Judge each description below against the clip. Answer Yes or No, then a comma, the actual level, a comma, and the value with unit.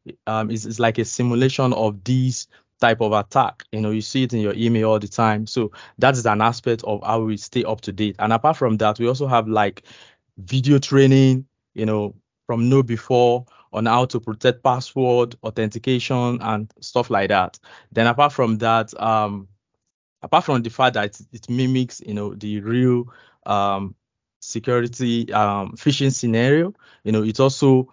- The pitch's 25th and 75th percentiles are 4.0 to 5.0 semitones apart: No, average, 2.8 semitones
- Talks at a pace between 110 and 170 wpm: No, average, 180 wpm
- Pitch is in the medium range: No, low, 115 Hz